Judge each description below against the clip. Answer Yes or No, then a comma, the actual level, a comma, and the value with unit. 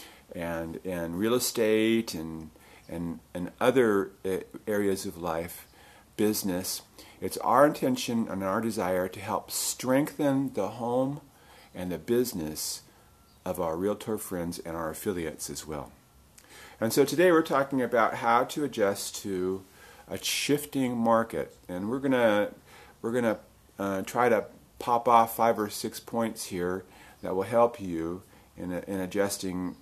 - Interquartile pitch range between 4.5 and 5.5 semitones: Yes, average, 5.0 semitones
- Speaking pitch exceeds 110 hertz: No, low, 105 Hz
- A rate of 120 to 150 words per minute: Yes, average, 140 wpm